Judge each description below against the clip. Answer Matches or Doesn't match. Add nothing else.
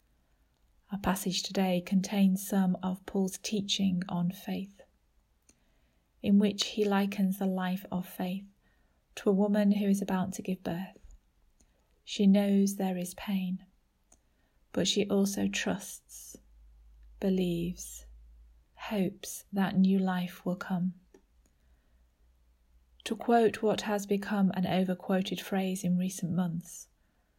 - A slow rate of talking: Matches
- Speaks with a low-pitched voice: Doesn't match